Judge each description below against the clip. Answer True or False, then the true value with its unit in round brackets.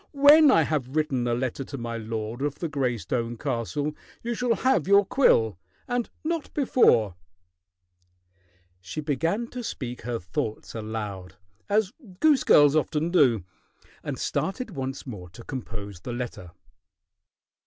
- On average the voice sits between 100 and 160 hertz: True (135 Hz)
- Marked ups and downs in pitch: True (8.9 semitones)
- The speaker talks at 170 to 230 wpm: False (145 wpm)